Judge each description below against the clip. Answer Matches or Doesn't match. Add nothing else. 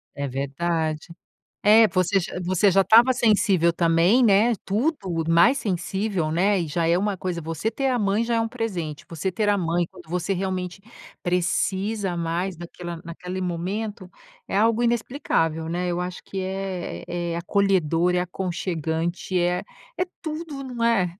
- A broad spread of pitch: Doesn't match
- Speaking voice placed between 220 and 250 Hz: Doesn't match